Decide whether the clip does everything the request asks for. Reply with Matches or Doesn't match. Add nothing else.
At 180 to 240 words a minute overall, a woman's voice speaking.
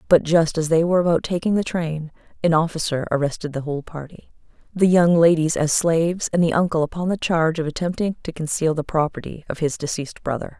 Matches